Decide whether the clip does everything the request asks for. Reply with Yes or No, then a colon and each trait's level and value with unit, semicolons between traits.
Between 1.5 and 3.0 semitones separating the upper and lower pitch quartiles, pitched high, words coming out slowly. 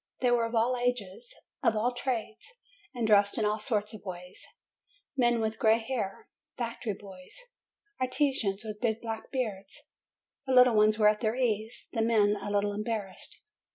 No: narrow, 2.6 semitones; high, 220 Hz; average, 165 wpm